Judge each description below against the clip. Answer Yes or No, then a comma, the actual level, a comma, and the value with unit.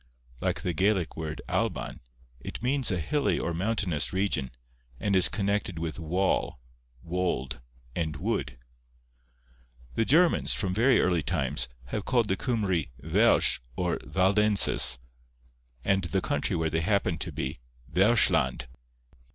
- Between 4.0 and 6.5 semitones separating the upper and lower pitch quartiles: Yes, average, 4.6 semitones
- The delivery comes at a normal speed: No, slow, 130 wpm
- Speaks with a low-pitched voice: Yes, very low, 90 Hz